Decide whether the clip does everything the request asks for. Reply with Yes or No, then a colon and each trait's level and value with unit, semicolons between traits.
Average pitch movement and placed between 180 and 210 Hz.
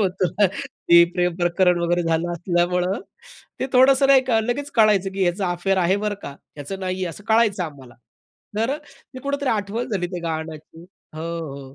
Yes: average, 3.9 semitones; medium, 185 Hz